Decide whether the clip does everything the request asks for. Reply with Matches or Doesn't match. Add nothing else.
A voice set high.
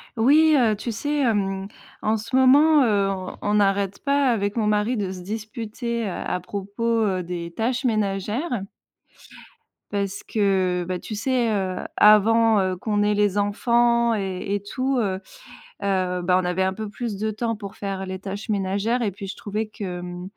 Matches